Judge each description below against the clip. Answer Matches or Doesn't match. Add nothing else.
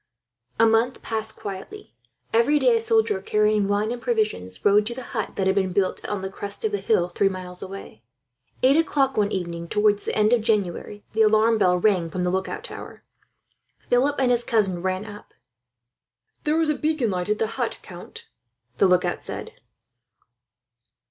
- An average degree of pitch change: Matches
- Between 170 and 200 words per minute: Matches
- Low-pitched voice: Doesn't match